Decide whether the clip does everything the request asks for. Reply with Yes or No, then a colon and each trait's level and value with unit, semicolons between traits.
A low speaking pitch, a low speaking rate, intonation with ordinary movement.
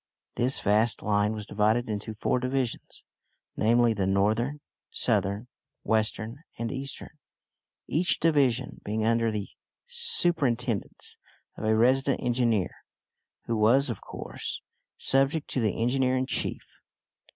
Yes: low, 115 Hz; slow, 120 wpm; average, 3.6 semitones